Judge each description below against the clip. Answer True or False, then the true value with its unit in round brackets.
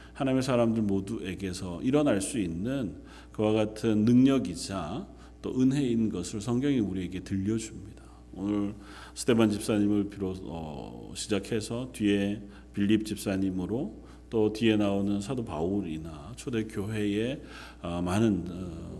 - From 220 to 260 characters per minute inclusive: False (280 characters per minute)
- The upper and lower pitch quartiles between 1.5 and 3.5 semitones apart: True (2.7 semitones)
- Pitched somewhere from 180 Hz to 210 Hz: False (105 Hz)